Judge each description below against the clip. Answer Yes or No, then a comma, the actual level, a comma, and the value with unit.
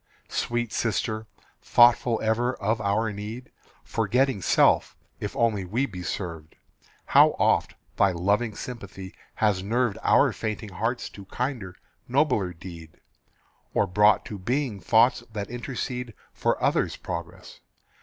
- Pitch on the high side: No, low, 110 Hz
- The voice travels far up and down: No, average, 3.5 semitones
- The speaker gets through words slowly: Yes, slow, 125 wpm